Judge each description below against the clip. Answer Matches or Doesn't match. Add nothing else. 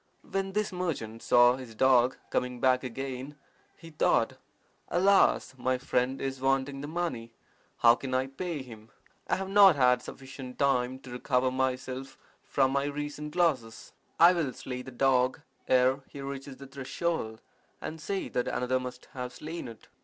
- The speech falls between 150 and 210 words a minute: Matches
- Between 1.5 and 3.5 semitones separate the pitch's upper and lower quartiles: Matches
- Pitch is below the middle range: Matches